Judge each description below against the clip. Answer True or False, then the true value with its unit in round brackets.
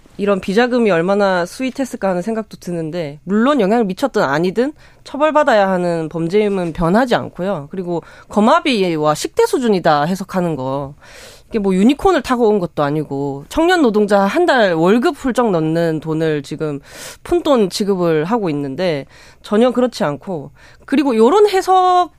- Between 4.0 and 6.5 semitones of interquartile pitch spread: False (7.0 semitones)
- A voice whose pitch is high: True (200 Hz)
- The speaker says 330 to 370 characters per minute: True (335 characters per minute)